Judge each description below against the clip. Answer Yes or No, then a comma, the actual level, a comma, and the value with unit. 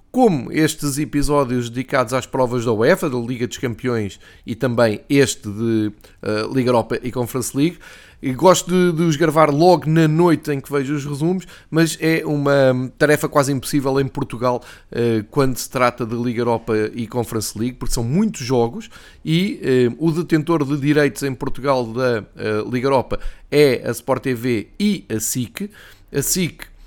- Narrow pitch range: No, average, 4.0 semitones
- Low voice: Yes, low, 130 Hz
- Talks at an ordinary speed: Yes, average, 165 wpm